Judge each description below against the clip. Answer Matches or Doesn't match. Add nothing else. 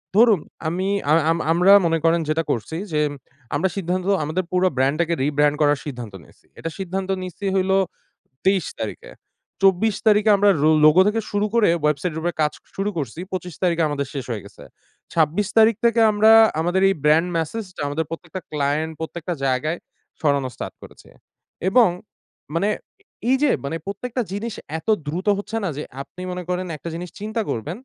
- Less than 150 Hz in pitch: Doesn't match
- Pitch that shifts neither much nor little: Matches